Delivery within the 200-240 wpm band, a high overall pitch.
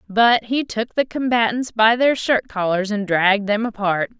No: average, 185 wpm; high, 220 Hz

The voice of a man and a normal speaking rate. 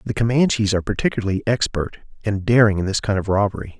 Yes: male; average, 190 wpm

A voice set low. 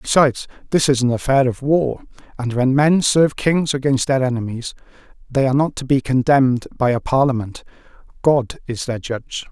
Yes: low, 130 Hz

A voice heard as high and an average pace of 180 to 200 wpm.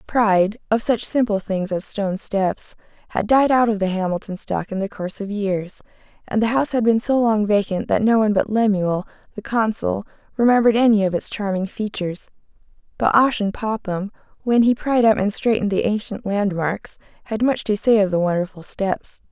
Yes: high, 210 Hz; average, 190 wpm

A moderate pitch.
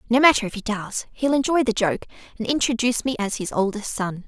No: high, 235 Hz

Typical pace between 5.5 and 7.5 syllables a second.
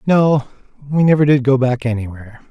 Yes: 5.8 syllables/s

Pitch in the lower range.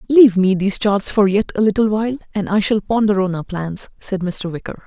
No: high, 200 Hz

